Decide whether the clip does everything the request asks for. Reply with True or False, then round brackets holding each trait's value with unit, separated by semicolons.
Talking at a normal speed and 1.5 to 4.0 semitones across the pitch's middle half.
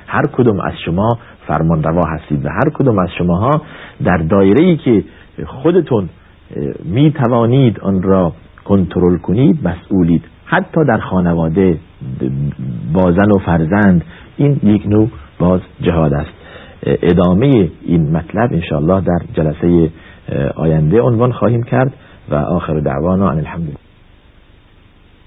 False (120 wpm; 4.4 semitones)